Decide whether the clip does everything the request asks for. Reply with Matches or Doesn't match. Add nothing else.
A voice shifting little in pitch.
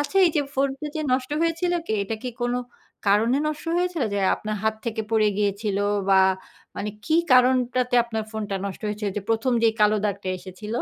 Doesn't match